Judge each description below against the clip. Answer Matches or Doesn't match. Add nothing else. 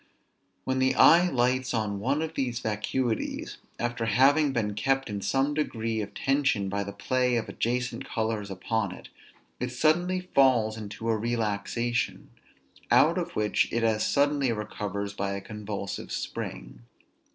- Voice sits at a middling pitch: Doesn't match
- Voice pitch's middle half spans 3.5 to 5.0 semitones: Matches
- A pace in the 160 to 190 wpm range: Doesn't match